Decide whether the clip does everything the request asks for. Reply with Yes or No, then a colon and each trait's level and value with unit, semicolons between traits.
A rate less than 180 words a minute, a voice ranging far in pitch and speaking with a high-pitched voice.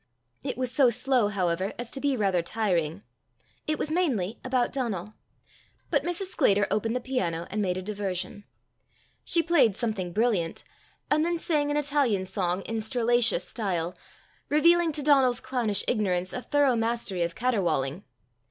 Yes: average, 155 wpm; wide, 6.1 semitones; high, 225 Hz